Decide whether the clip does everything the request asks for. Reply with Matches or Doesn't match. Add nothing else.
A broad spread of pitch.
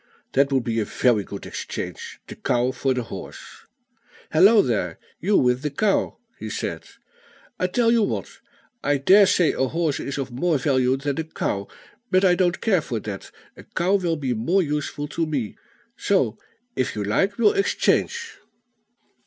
Matches